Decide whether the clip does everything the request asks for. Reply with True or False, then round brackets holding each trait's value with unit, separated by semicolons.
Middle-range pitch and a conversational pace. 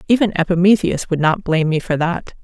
True (175 Hz; 195 wpm)